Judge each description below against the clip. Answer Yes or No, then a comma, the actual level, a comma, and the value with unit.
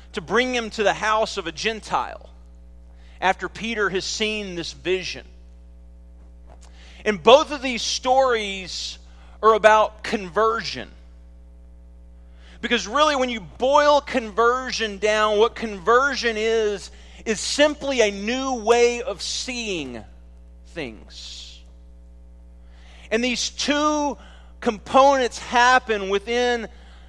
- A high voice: Yes, high, 210 Hz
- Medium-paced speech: No, slow, 105 wpm